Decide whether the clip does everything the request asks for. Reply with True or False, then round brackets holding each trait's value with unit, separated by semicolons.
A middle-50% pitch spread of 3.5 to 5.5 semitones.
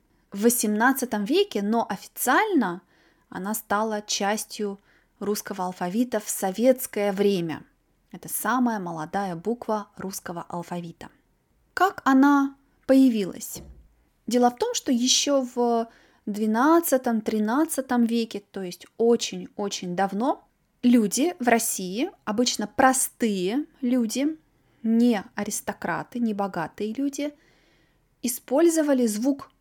True (4.6 semitones)